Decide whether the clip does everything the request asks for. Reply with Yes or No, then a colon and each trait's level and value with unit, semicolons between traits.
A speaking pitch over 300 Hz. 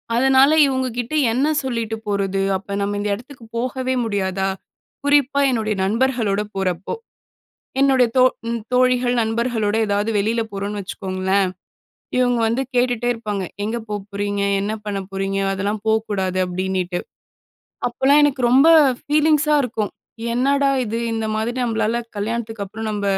No: high, 225 Hz